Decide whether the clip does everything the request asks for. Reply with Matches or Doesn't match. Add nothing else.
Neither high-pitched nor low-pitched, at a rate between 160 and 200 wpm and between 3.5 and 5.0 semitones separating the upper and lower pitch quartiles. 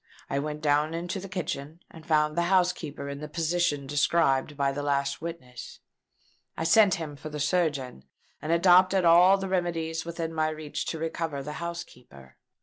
Doesn't match